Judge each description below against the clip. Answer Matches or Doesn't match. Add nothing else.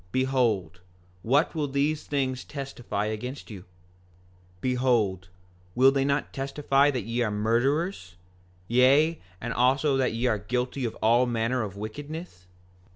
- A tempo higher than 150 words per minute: Doesn't match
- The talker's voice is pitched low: Matches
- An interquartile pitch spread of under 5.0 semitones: Matches